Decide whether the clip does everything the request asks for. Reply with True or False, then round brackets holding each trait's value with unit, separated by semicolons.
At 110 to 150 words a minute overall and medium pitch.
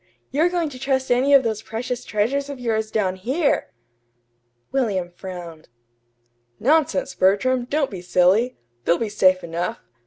False (145 wpm; 230 Hz)